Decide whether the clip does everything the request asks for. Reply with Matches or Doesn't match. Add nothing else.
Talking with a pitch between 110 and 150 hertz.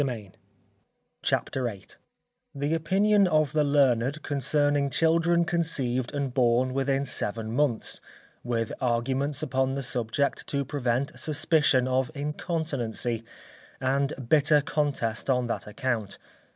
Matches